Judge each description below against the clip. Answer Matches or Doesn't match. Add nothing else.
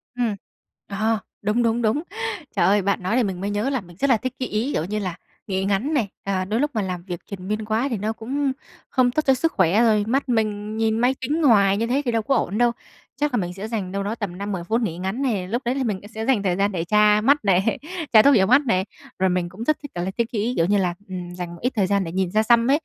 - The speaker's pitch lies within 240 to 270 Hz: Doesn't match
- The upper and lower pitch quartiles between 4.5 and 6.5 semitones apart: Doesn't match